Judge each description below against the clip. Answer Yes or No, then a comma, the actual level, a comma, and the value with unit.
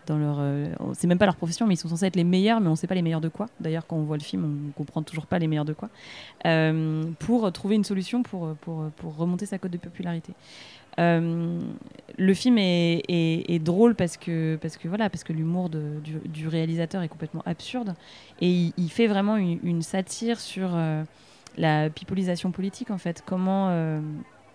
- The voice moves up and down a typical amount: Yes, average, 3.1 semitones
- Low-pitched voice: No, medium, 170 Hz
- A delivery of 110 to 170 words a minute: No, fast, 220 wpm